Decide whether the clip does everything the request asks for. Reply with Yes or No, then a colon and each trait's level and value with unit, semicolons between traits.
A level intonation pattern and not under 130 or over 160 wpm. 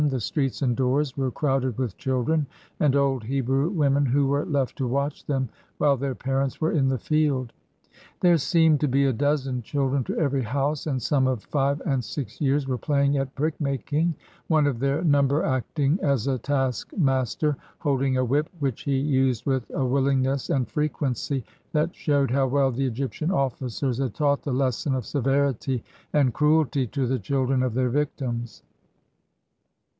No: narrow, 1.8 semitones; average, 175 wpm